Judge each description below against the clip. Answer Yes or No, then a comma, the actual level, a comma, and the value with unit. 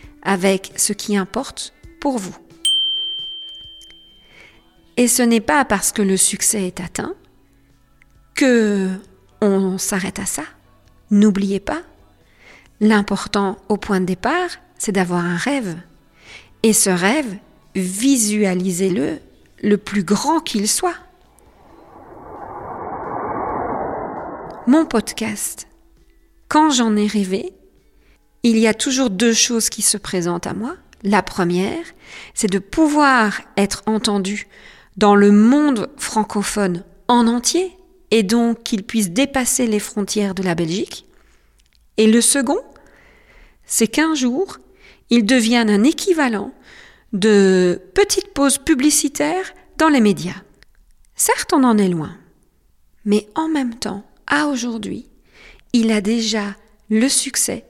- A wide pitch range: Yes, wide, 5.7 semitones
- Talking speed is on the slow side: Yes, slow, 120 wpm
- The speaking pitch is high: Yes, high, 220 Hz